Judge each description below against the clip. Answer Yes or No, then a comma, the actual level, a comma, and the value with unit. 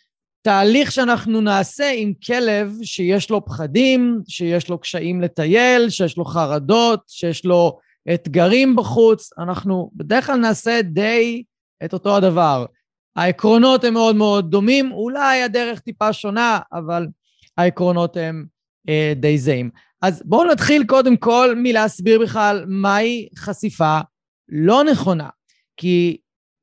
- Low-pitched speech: No, high, 205 Hz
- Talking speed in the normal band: Yes, average, 120 wpm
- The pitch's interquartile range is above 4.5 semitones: Yes, average, 5.0 semitones